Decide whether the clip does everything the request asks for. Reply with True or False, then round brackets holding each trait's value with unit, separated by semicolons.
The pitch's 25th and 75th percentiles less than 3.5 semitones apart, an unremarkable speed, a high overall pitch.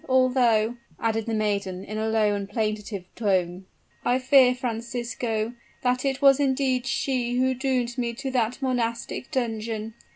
True (2.9 semitones; 150 wpm; 235 Hz)